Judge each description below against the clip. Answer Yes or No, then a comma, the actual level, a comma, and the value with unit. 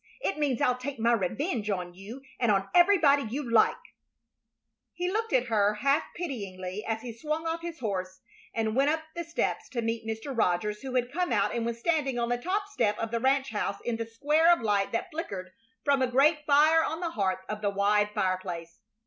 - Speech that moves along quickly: Yes, fast, 210 wpm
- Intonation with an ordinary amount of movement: No, wide, 6.2 semitones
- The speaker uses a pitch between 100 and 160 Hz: No, high, 235 Hz